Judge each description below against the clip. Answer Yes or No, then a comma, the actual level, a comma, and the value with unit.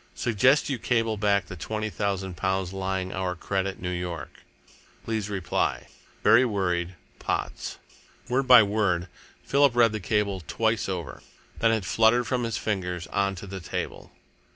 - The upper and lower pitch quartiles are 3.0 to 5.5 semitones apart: Yes, average, 3.3 semitones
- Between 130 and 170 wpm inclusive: Yes, average, 150 wpm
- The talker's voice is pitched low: Yes, low, 100 Hz